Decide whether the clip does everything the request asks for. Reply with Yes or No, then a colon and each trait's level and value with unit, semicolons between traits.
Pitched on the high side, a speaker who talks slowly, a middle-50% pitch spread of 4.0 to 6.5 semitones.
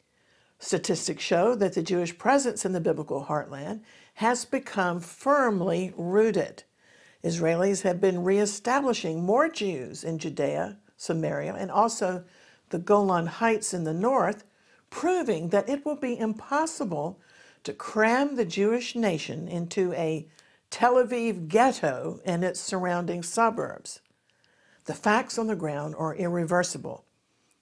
Yes: high, 195 Hz; slow, 125 wpm; average, 5.1 semitones